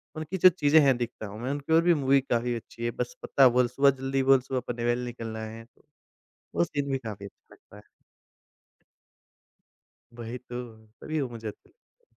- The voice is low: Yes, low, 125 Hz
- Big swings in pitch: No, average, 3.2 semitones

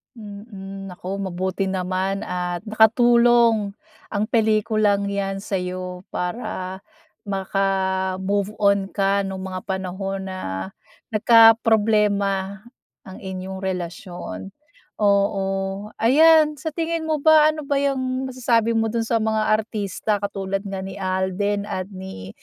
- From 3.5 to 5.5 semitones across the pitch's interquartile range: No, average, 2.9 semitones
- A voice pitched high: Yes, high, 200 Hz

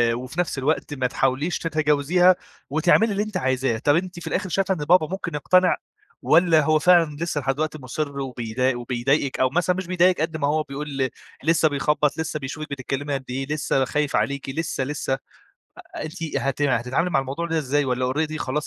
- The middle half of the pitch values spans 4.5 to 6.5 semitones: No, average, 3.7 semitones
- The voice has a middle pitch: Yes, medium, 150 Hz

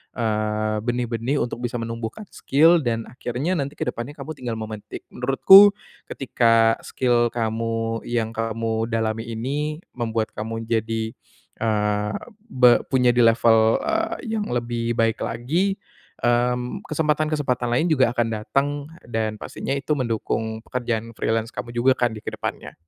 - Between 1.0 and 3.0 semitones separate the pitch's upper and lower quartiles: Yes, average, 2.7 semitones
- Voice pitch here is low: Yes, low, 120 Hz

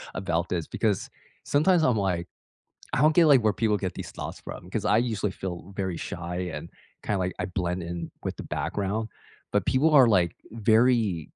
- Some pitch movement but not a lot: Yes, average, 4.5 semitones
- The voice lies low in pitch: Yes, low, 100 Hz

